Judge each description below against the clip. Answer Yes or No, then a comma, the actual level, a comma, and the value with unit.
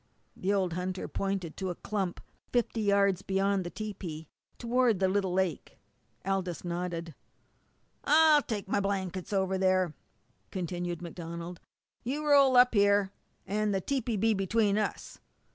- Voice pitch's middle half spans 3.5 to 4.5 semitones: No, average, 2.8 semitones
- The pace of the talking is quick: No, average, 145 wpm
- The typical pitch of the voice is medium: No, high, 195 Hz